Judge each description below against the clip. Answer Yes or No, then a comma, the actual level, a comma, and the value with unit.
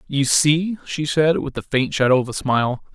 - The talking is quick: Yes, fast, 225 wpm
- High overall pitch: No, medium, 145 Hz